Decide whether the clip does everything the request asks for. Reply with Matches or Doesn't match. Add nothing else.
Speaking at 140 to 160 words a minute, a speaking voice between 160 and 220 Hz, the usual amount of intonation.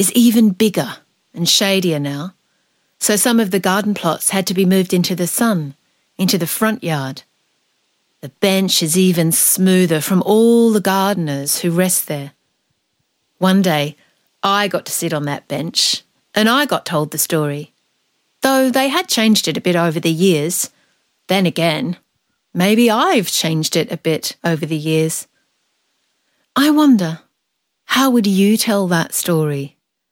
Matches